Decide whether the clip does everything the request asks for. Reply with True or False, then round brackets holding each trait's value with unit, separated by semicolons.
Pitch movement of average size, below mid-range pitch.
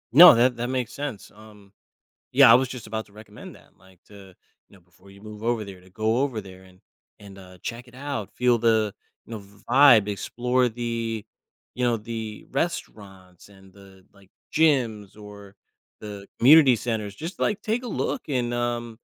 True (3.7 semitones; 110 Hz)